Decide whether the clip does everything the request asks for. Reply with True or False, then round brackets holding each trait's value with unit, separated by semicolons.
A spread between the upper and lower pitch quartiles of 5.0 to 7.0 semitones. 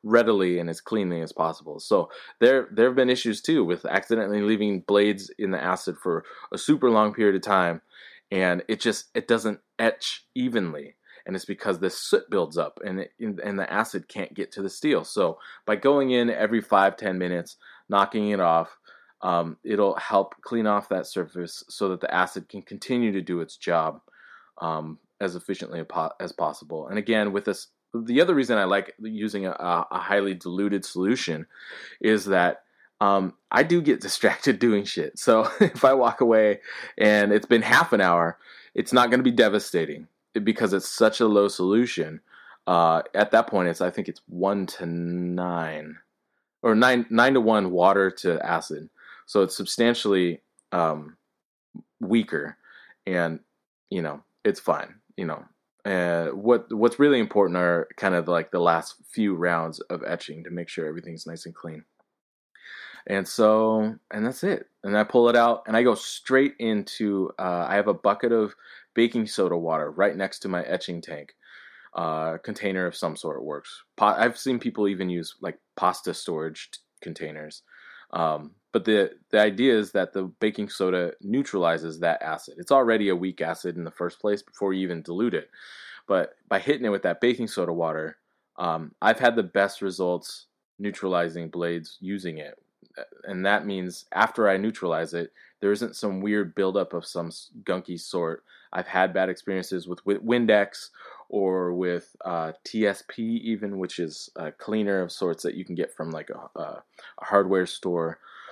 False (3.7 semitones)